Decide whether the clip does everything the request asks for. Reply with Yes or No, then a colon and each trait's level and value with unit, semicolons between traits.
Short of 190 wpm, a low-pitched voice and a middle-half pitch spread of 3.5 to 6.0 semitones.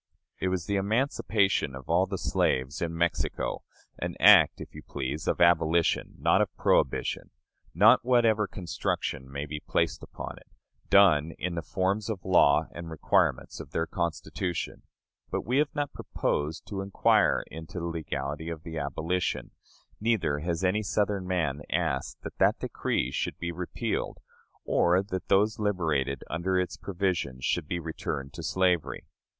Yes: average, 155 wpm; very low, 85 Hz; average, 3.8 semitones